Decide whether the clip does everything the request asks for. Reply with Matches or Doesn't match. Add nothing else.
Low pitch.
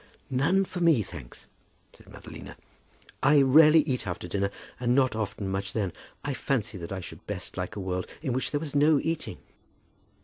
Matches